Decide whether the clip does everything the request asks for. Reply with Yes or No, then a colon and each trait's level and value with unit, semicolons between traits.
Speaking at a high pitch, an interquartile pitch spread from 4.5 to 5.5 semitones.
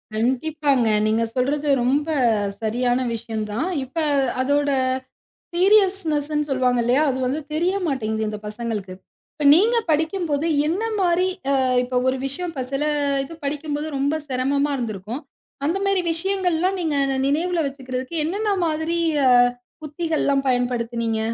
Yes: very high, 285 Hz; average, 4.8 semitones